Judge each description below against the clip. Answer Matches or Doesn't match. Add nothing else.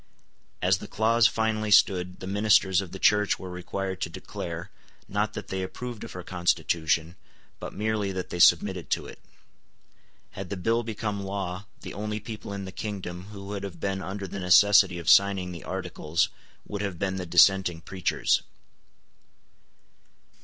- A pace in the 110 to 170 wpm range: Matches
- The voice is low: Matches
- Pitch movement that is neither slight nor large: Doesn't match